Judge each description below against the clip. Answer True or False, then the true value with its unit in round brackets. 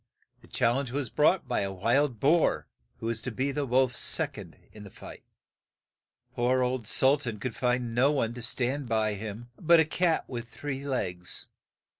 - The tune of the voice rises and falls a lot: False (3.4 semitones)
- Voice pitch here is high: False (125 Hz)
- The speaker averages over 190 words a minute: True (200 wpm)